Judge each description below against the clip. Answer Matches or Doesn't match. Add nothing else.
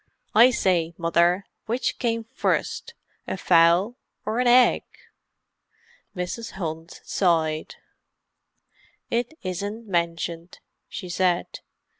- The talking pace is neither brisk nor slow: Doesn't match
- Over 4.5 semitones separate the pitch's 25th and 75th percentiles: Matches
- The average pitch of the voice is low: Doesn't match